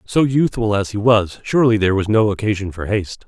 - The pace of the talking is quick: Yes, fast, 220 wpm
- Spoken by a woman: No, male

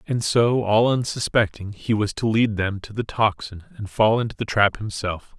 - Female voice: No, male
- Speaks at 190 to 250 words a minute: Yes, average, 200 wpm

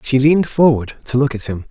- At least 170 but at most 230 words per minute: No, fast, 245 wpm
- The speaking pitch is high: No, low, 130 Hz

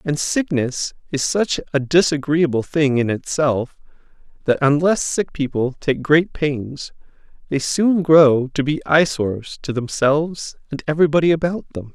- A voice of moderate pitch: Yes, medium, 150 Hz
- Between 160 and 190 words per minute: No, average, 140 wpm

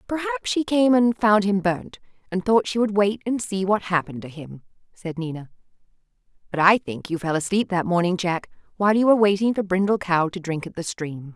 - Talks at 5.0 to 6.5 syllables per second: Yes, 5.5 syllables/s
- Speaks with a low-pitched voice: No, high, 195 Hz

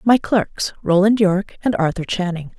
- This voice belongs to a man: No, female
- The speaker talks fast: No, average, 140 wpm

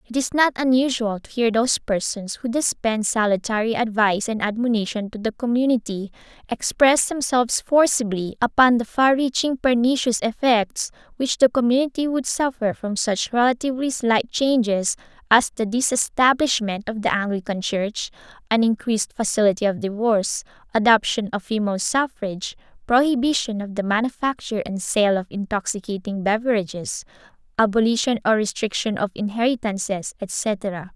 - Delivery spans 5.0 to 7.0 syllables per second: Yes, 5.2 syllables/s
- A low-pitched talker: No, high, 225 Hz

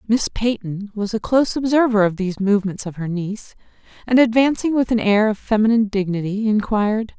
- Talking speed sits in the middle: Yes, average, 175 wpm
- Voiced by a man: No, female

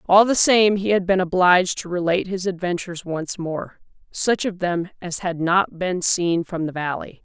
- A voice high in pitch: No, medium, 180 Hz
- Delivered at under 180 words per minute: No, average, 200 wpm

